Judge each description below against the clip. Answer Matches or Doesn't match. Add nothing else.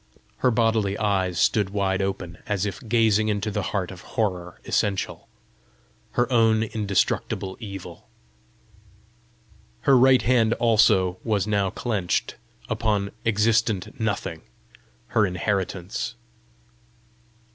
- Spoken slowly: Matches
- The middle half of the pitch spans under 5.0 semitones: Matches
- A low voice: Matches